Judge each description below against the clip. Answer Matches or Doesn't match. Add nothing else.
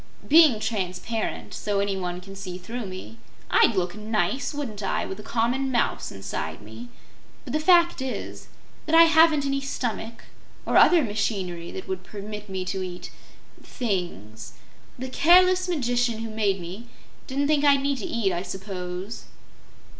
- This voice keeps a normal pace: Matches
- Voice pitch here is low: Doesn't match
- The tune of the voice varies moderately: Doesn't match